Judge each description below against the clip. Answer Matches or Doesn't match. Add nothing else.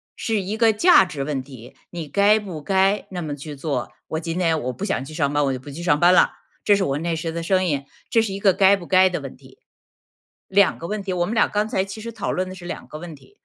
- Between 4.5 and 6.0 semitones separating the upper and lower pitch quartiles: Matches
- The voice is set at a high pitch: Doesn't match